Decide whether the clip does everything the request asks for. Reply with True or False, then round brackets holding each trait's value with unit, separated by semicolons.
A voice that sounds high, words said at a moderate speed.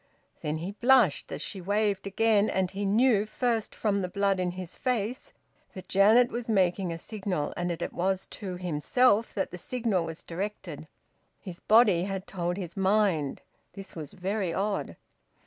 True (195 Hz; 170 wpm)